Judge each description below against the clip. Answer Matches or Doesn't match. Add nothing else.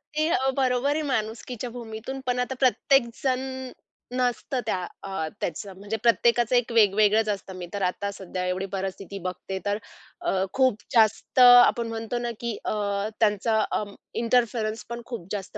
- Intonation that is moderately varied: Matches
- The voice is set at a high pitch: Matches